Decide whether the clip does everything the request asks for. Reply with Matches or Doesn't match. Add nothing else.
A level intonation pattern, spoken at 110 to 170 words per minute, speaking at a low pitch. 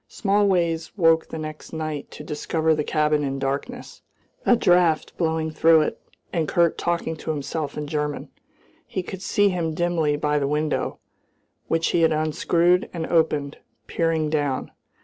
Doesn't match